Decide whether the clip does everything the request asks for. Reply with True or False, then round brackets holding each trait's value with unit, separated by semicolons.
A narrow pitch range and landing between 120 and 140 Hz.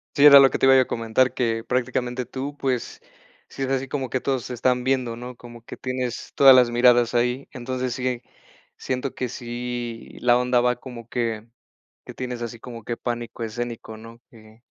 True (1.4 semitones; 125 Hz)